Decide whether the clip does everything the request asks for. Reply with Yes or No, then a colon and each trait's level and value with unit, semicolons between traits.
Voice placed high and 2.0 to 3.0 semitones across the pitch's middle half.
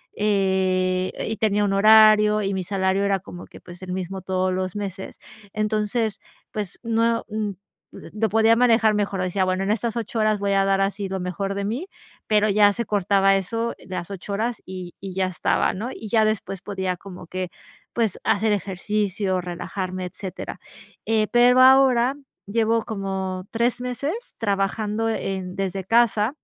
Yes: high, 200 Hz; narrow, 2.6 semitones